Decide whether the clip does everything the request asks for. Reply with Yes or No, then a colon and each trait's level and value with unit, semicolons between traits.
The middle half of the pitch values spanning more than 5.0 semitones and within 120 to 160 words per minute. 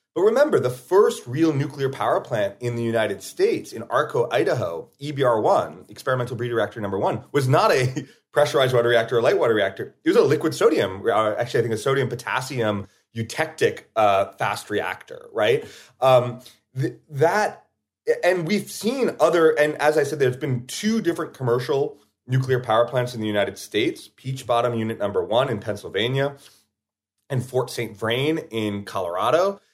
No: wide, 5.4 semitones; average, 170 wpm